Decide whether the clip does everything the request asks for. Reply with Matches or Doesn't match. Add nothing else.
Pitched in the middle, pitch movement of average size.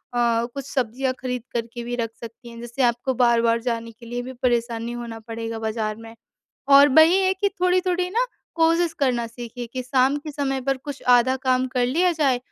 Doesn't match